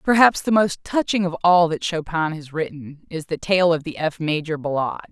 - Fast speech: Yes, fast, 210 wpm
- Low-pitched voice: No, medium, 165 Hz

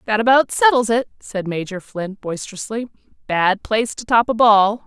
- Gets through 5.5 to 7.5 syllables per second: No, 5.0 syllables/s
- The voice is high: Yes, high, 220 Hz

